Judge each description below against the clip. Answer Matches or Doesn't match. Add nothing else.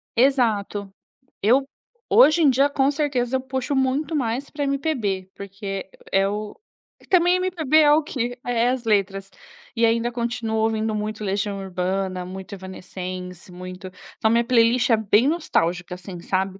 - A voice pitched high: Matches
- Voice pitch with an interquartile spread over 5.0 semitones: Matches